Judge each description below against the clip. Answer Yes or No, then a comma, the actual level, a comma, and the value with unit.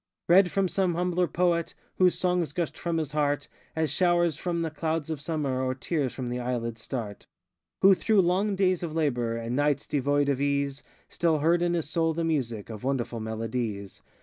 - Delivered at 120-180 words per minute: No, average, 190 wpm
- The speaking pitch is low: No, medium, 155 Hz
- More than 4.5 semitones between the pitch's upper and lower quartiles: Yes, average, 5.1 semitones